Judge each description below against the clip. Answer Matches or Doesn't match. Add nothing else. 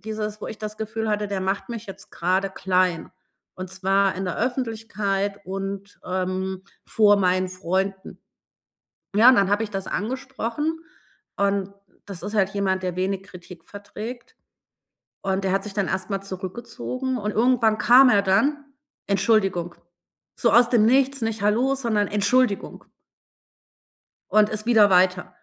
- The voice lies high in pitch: Matches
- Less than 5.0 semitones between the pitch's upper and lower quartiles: Matches